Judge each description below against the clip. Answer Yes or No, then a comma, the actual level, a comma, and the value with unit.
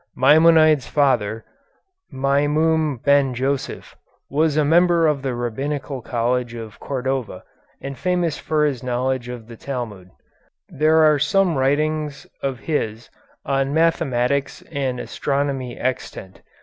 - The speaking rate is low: Yes, slow, 120 wpm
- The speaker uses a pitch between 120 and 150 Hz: Yes, medium, 140 Hz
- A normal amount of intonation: Yes, average, 3.5 semitones